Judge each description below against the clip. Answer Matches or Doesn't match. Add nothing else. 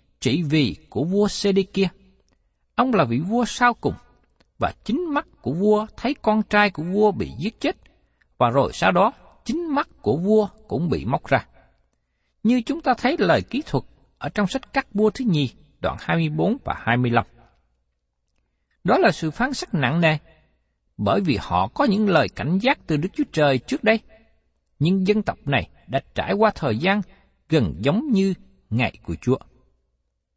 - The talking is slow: Doesn't match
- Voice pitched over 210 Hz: Doesn't match